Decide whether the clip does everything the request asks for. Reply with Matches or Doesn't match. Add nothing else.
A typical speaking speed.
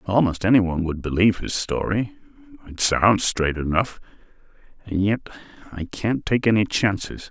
Doesn't match